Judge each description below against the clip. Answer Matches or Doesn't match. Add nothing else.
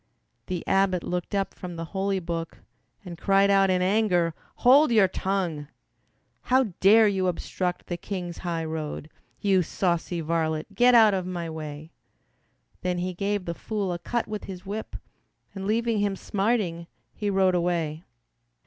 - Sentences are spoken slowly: Doesn't match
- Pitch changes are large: Doesn't match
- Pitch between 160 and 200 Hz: Matches